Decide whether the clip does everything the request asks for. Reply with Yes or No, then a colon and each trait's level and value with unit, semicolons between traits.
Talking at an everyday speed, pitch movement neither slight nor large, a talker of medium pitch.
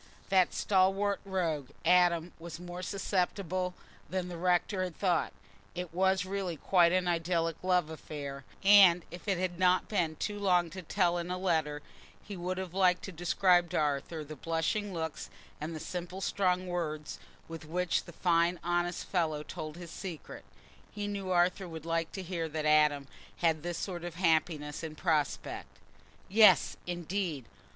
No: average, 165 wpm; narrow, 2.3 semitones; medium, 175 Hz